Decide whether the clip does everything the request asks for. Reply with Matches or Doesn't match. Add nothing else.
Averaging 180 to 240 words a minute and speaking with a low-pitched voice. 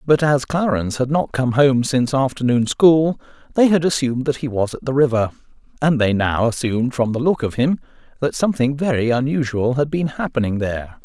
Matches